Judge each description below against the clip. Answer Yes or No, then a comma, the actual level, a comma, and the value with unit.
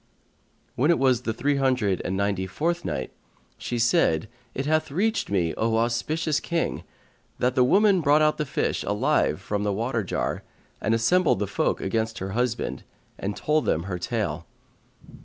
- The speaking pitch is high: No, low, 120 Hz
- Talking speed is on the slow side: No, average, 170 wpm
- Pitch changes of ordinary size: No, wide, 6.7 semitones